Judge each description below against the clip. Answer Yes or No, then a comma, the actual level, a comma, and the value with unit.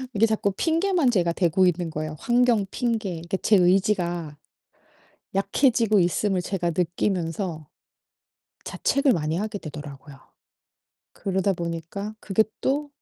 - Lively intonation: No, average, 4.4 semitones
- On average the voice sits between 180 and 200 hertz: Yes, high, 190 Hz